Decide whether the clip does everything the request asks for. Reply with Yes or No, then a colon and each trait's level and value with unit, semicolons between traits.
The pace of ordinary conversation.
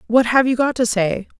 No: fast, 255 wpm